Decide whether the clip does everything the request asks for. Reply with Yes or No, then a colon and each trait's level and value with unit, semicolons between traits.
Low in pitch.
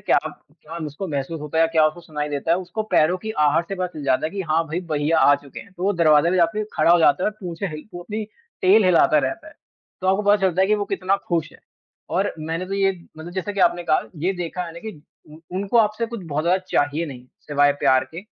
No: medium, 170 Hz